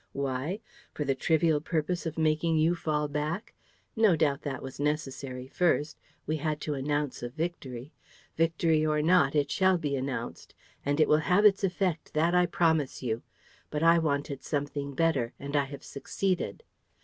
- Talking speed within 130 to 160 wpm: No, average, 170 wpm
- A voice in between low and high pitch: Yes, medium, 150 Hz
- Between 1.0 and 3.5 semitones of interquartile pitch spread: Yes, average, 2.9 semitones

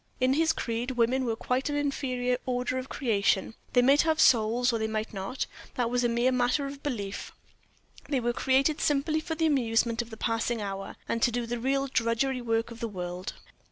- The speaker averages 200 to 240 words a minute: Yes, fast, 205 wpm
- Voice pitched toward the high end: Yes, high, 245 Hz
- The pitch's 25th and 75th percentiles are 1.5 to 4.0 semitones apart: Yes, average, 2.8 semitones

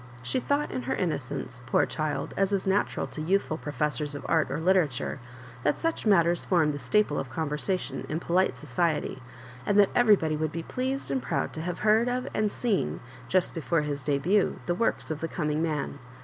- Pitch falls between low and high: Yes, medium, 165 Hz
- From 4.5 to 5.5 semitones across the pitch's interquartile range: Yes, average, 5.0 semitones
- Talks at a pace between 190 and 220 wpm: Yes, average, 195 wpm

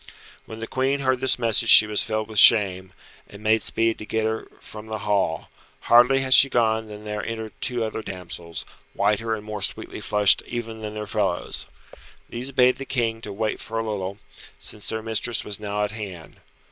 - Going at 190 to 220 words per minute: Yes, average, 195 wpm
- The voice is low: Yes, low, 110 Hz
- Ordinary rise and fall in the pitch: No, narrow, 1.6 semitones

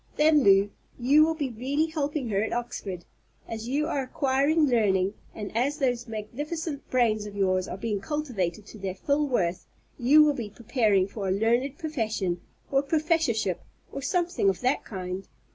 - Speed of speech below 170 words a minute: No, average, 175 wpm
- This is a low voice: No, high, 240 Hz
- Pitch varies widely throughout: Yes, wide, 6.4 semitones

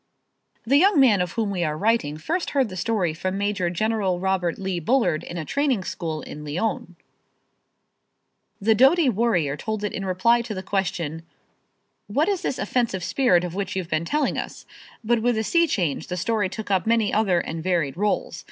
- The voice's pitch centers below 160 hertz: No, high, 195 Hz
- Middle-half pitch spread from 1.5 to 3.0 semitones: No, average, 4.7 semitones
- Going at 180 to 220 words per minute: Yes, average, 190 wpm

